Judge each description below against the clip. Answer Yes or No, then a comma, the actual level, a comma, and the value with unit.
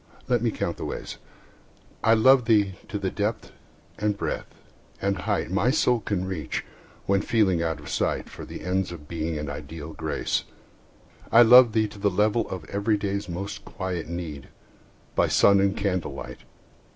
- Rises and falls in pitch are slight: No, average, 3.9 semitones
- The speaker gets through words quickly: No, average, 165 wpm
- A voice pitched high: No, low, 100 Hz